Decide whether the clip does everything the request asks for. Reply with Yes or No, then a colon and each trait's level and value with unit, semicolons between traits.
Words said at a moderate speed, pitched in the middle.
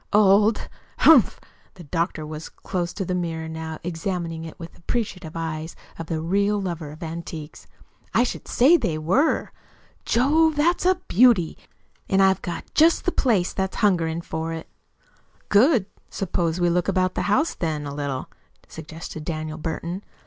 Yes: average, 165 wpm; medium, 175 Hz